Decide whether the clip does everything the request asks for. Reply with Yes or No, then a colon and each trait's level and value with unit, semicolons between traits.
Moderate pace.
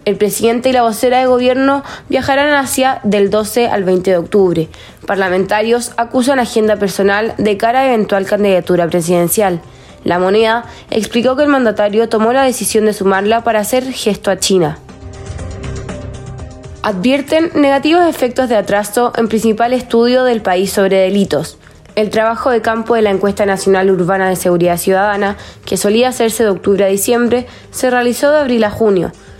Yes: average, 160 wpm